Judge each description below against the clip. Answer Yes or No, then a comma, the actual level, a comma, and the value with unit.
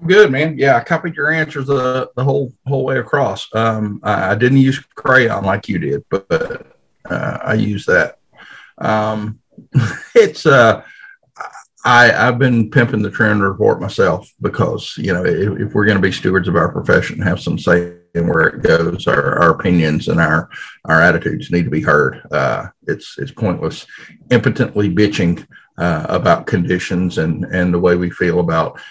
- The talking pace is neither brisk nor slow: Yes, average, 175 wpm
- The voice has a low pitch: Yes, low, 110 Hz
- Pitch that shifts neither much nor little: No, wide, 7.2 semitones